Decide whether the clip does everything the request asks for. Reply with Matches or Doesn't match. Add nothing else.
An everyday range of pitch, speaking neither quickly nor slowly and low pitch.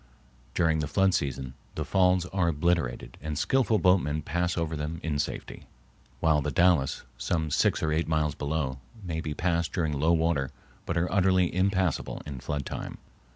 Matches